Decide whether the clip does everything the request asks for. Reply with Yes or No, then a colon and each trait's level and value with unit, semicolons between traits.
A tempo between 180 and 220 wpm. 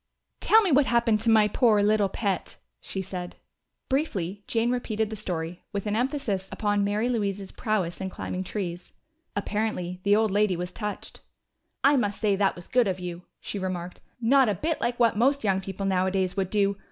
Yes: average, 190 wpm